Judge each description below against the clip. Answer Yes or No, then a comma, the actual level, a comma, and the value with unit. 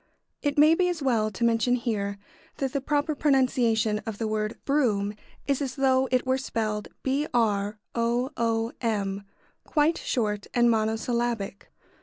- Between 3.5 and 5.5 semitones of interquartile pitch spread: Yes, average, 3.8 semitones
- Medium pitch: No, high, 235 Hz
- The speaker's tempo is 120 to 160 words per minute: Yes, average, 140 wpm